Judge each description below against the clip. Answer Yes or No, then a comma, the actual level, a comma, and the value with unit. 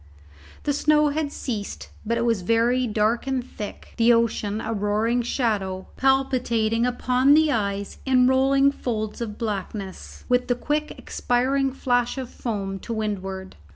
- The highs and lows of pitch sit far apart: No, average, 3.7 semitones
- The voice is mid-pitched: No, high, 235 Hz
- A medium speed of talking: Yes, average, 150 wpm